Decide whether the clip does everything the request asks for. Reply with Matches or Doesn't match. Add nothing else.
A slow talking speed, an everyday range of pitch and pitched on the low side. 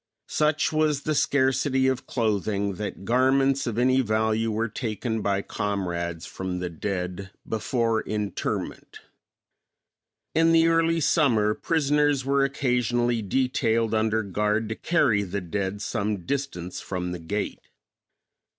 Matches